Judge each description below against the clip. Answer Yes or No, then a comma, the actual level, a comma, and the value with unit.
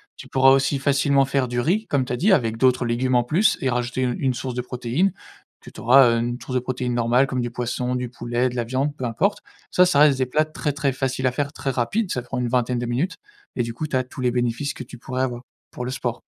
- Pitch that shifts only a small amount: Yes, narrow, 2.1 semitones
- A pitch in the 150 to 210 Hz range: No, low, 130 Hz